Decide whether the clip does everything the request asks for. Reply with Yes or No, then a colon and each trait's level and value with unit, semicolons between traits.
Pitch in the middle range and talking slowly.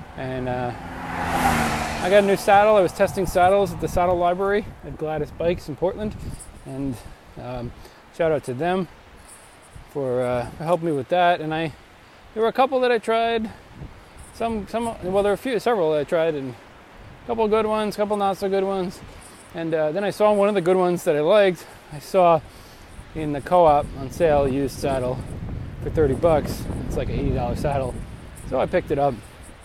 No: medium, 165 Hz; average, 200 wpm